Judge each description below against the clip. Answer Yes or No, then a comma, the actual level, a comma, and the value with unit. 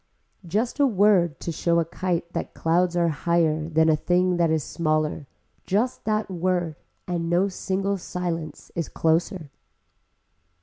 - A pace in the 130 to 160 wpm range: Yes, average, 145 wpm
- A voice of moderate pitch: Yes, medium, 170 Hz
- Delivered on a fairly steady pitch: Yes, narrow, 2.3 semitones